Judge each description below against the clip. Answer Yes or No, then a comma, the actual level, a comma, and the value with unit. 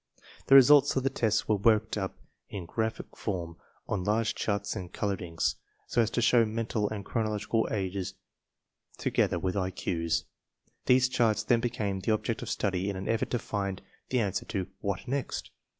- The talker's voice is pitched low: Yes, low, 105 Hz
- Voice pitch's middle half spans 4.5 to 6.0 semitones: No, average, 3.1 semitones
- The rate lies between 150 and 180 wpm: Yes, average, 175 wpm